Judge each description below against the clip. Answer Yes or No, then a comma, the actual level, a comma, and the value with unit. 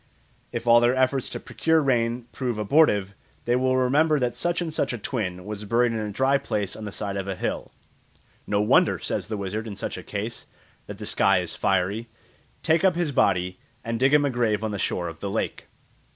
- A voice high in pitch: No, low, 115 Hz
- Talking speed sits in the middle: No, fast, 220 wpm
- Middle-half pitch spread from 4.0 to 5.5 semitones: Yes, average, 4.5 semitones